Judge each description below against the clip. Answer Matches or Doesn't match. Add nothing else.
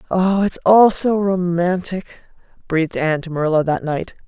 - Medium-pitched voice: Matches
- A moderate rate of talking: Matches